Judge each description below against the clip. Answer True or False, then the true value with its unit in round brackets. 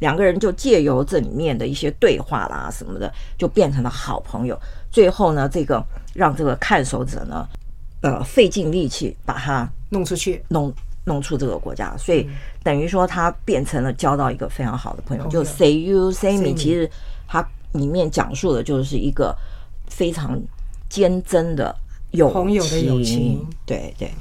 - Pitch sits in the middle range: True (150 Hz)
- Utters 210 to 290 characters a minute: True (265 characters per minute)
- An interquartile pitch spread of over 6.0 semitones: False (5.1 semitones)